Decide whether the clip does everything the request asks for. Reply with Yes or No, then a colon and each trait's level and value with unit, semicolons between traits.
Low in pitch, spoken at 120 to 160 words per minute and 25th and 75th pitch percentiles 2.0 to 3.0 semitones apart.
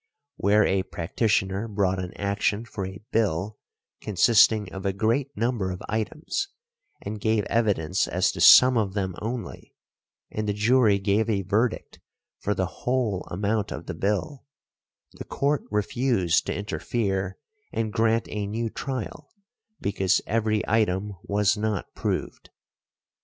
Yes: low, 105 Hz; average, 140 wpm; narrow, 2.6 semitones